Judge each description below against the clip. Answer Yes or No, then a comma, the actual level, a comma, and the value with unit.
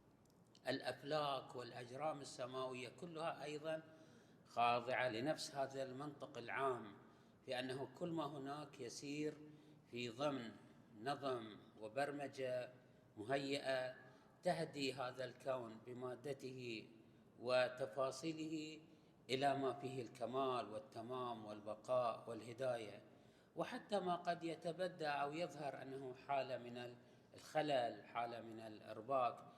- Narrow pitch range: No, average, 3.3 semitones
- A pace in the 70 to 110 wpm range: Yes, average, 95 wpm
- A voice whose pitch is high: No, low, 130 Hz